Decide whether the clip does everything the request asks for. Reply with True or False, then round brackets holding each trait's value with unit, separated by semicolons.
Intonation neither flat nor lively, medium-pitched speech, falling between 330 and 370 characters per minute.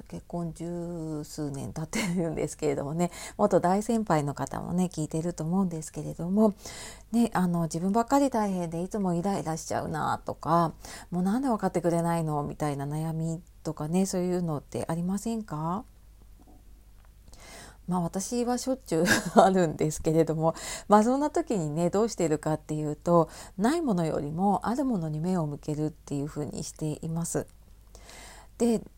True (4.2 semitones; 170 Hz; 350 characters per minute)